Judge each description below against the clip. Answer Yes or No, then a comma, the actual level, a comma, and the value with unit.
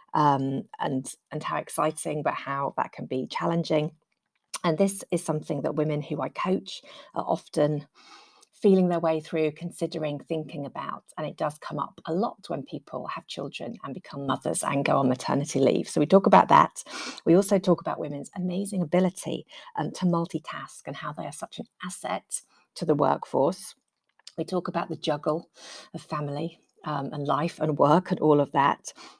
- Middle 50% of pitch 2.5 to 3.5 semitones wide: Yes, average, 2.8 semitones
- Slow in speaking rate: No, average, 185 wpm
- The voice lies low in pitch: No, medium, 160 Hz